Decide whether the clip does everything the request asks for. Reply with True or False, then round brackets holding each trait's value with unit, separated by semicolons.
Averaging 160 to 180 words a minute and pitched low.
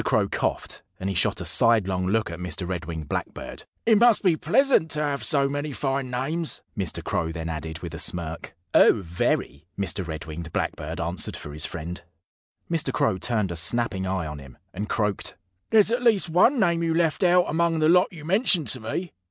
False (200 wpm; 115 Hz)